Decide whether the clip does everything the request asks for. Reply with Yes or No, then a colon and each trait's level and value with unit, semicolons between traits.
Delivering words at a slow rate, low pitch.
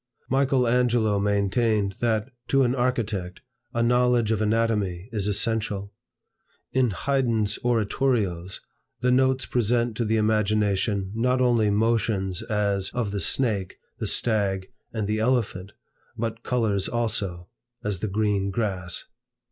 Yes: slow, 125 wpm; low, 110 Hz